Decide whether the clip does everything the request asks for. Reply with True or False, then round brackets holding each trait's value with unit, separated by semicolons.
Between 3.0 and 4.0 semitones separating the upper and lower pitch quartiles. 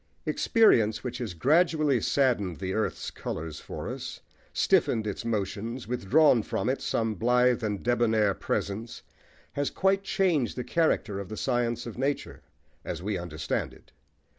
False (4.5 semitones)